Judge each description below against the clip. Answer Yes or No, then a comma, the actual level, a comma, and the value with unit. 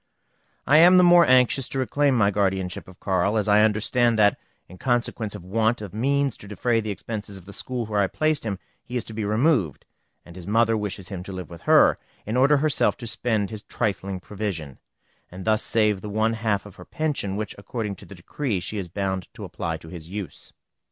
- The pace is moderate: No, fast, 220 wpm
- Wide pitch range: No, average, 3.8 semitones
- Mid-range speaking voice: No, low, 105 Hz